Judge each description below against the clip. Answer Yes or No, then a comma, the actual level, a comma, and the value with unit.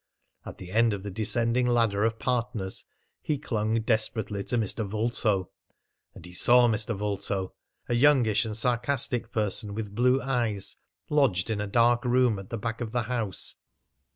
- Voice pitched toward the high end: No, low, 115 Hz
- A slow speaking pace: No, average, 165 wpm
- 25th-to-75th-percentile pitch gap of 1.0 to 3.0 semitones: Yes, average, 2.7 semitones